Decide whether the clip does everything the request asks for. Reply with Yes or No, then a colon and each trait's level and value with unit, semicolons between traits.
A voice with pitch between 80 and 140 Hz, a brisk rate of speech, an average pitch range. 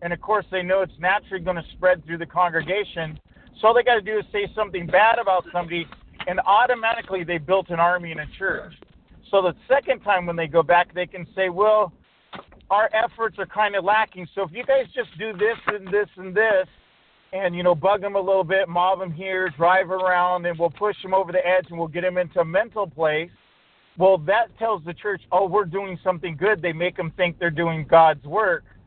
No: medium, 185 Hz; fast, 225 wpm; average, 3.0 semitones